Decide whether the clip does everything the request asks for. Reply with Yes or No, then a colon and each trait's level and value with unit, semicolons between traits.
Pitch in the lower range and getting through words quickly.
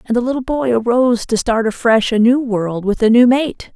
No: high, 235 Hz; fast, 240 wpm